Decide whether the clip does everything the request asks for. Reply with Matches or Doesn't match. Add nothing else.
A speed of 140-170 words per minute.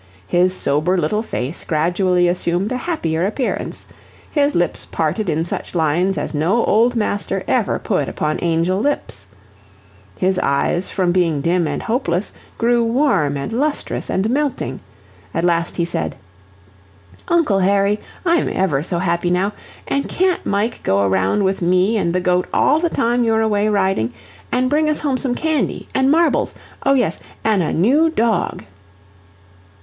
Matches